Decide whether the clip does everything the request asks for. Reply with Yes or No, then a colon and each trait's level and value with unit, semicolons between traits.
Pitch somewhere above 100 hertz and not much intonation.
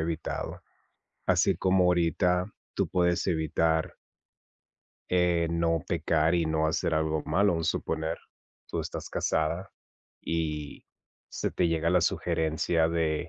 No: very low, 80 Hz; narrow, 1.7 semitones